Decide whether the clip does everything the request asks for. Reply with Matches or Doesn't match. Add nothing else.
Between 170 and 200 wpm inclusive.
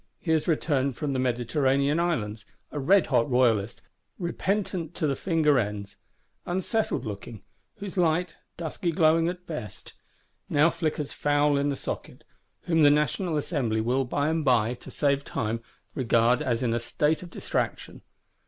Doesn't match